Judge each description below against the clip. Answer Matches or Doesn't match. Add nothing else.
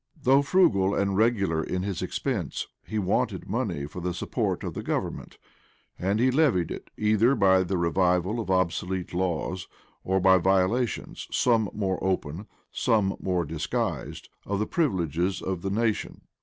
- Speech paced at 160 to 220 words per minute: Doesn't match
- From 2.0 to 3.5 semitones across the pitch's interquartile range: Matches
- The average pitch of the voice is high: Doesn't match